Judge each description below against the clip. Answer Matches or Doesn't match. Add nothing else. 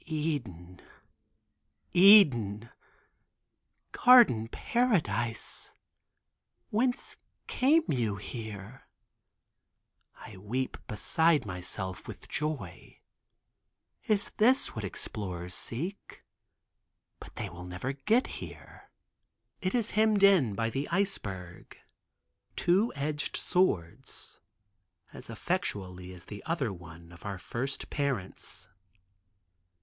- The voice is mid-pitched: Doesn't match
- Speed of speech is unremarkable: Doesn't match